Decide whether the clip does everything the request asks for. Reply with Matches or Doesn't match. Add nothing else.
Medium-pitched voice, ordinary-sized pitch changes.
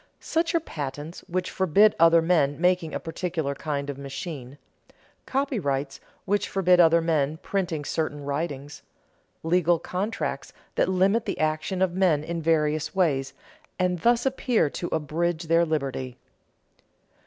Matches